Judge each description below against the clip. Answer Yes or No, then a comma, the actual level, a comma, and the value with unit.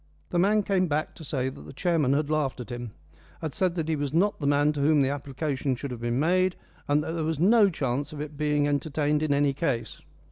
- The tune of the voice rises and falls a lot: No, average, 2.7 semitones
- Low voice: No, medium, 150 Hz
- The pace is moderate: No, fast, 245 wpm